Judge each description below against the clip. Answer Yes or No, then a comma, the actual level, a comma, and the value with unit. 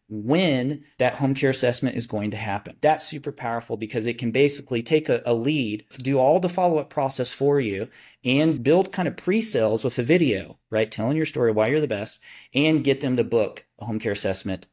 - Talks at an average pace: No, fast, 220 wpm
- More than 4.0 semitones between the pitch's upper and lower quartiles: Yes, average, 4.8 semitones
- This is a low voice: Yes, low, 130 Hz